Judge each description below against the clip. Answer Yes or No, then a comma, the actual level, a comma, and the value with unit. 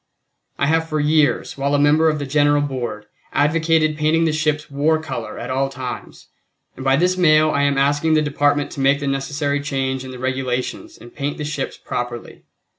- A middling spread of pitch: No, narrow, 2.3 semitones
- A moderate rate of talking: Yes, average, 195 wpm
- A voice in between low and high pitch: Yes, medium, 145 Hz